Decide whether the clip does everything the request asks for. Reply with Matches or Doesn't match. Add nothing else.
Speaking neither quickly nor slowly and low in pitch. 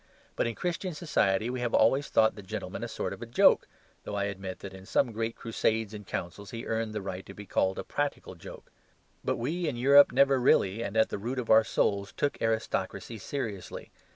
Doesn't match